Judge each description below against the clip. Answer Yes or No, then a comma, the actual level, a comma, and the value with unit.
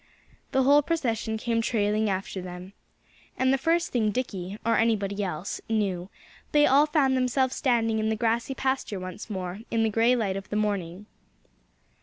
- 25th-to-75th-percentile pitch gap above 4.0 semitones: Yes, average, 4.5 semitones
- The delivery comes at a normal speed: Yes, average, 170 wpm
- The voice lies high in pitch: Yes, high, 220 Hz